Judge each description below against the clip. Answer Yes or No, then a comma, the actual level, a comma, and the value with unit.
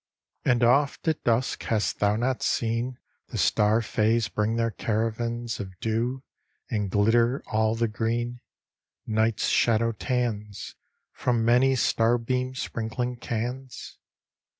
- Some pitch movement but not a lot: No, narrow, 1.8 semitones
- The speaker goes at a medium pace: No, slow, 120 wpm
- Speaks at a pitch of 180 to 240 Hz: No, low, 115 Hz